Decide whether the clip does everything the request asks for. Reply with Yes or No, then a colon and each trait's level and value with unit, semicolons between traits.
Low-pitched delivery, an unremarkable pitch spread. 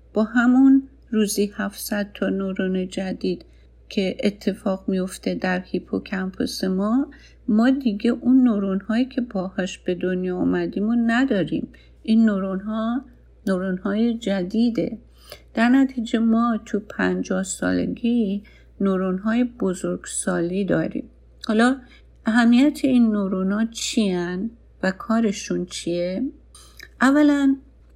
No: high, 210 Hz; average, 4.0 semitones